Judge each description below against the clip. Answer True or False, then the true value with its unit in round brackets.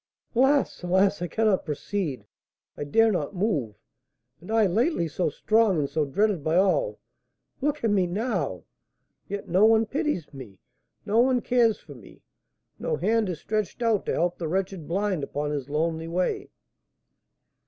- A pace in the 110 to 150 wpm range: False (160 wpm)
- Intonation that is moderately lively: False (5.7 semitones)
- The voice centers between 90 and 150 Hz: False (190 Hz)